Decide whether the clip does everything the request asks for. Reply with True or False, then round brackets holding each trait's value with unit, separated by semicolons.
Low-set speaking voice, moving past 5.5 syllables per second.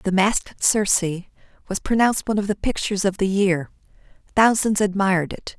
False (200 Hz; 5.9 syllables/s)